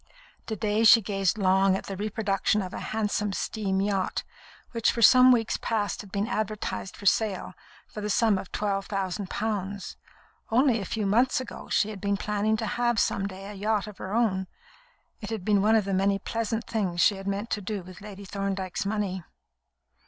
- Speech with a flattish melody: Yes, narrow, 2.0 semitones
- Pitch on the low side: No, high, 205 Hz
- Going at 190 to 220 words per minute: Yes, average, 195 wpm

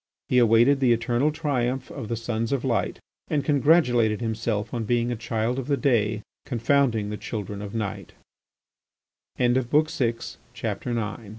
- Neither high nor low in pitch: No, low, 120 Hz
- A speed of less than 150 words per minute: Yes, average, 140 wpm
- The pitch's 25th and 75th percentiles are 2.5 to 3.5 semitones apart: Yes, average, 2.9 semitones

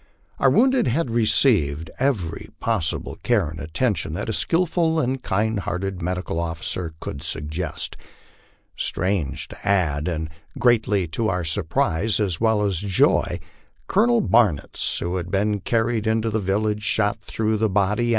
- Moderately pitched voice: No, low, 100 Hz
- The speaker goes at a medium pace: Yes, average, 160 wpm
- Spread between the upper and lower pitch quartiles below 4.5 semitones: No, average, 5.0 semitones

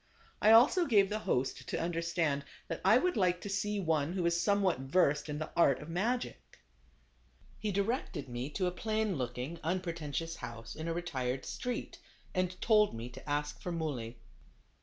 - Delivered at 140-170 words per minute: No, average, 180 wpm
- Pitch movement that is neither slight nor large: No, wide, 5.7 semitones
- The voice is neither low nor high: Yes, medium, 170 Hz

